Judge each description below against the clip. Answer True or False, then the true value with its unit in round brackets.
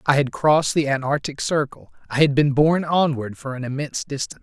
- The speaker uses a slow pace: False (205 wpm)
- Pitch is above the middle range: False (145 Hz)